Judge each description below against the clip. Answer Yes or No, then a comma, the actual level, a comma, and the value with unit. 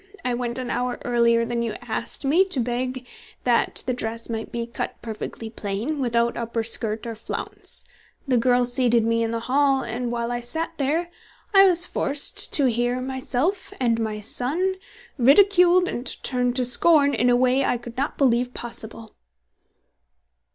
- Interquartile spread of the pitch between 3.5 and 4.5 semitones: No, average, 2.7 semitones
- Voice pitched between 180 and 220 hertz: No, high, 245 Hz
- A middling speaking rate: Yes, average, 170 wpm